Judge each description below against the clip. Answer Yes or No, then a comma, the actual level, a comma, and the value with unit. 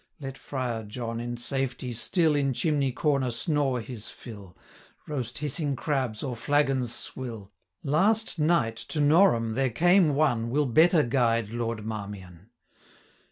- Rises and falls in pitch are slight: No, average, 4.3 semitones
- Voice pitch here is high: No, low, 130 Hz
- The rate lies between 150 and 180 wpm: No, average, 140 wpm